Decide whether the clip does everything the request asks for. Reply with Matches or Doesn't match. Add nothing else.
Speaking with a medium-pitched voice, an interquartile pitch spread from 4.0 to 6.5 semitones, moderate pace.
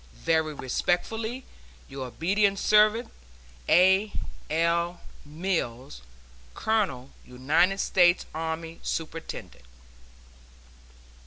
Doesn't match